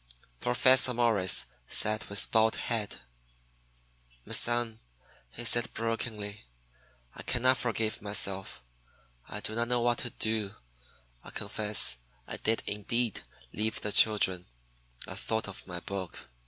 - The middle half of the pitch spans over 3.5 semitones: No, narrow, 2.4 semitones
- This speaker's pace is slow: Yes, slow, 130 wpm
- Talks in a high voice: No, low, 110 Hz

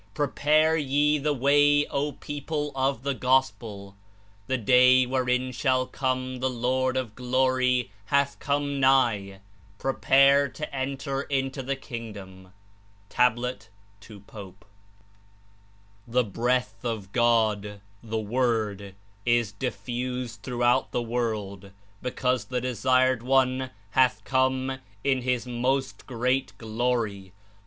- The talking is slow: Yes, slow, 115 wpm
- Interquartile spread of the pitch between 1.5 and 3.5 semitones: Yes, average, 2.7 semitones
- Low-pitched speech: Yes, low, 125 Hz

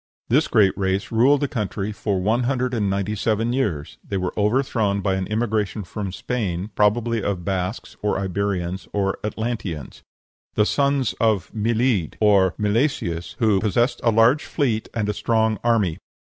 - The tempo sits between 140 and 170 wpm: Yes, average, 160 wpm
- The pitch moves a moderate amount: Yes, average, 3.3 semitones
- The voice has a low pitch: Yes, low, 105 Hz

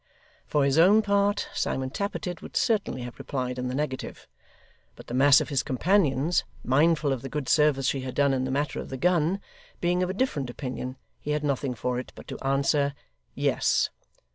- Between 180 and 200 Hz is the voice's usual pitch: No, medium, 140 Hz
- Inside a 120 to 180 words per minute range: No, average, 195 wpm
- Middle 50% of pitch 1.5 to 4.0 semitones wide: No, average, 4.6 semitones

